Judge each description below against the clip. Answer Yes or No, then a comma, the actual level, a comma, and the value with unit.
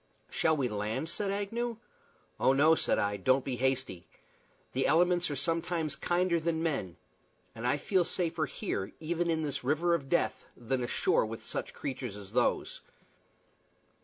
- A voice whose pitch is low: No, medium, 150 Hz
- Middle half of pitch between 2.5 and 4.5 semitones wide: No, average, 5.3 semitones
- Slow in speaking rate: No, average, 160 wpm